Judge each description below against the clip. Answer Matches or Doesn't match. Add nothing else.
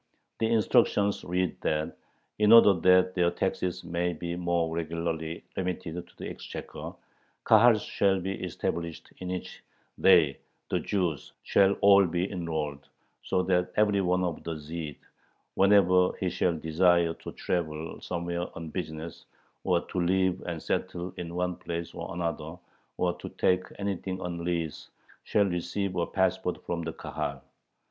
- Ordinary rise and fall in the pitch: Doesn't match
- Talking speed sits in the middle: Matches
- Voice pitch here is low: Matches